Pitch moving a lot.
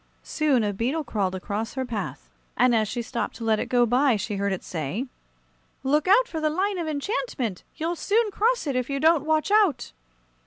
Yes: wide, 6.4 semitones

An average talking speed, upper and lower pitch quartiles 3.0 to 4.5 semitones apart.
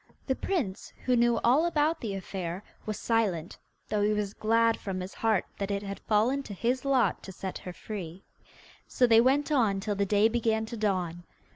Yes: average, 195 wpm; average, 3.6 semitones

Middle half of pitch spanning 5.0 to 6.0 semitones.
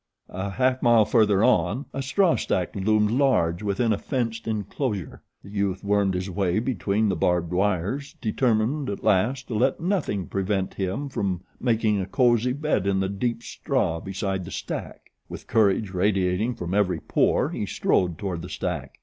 No: average, 4.2 semitones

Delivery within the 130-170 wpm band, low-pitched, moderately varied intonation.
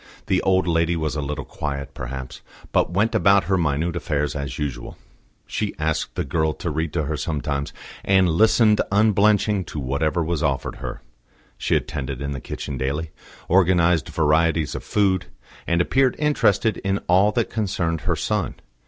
Yes: average, 165 wpm; very low, 80 Hz; average, 4.6 semitones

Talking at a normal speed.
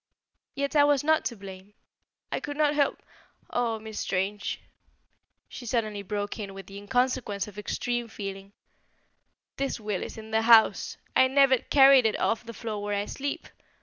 Yes: average, 170 wpm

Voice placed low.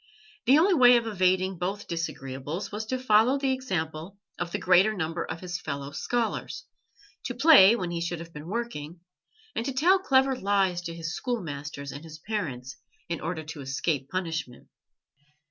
No: medium, 180 Hz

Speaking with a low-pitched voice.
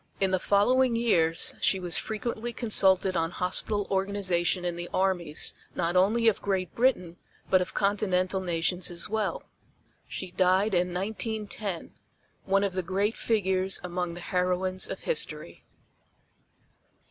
No: high, 190 Hz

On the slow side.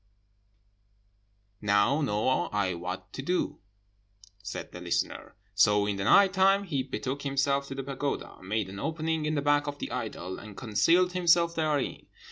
No: average, 160 wpm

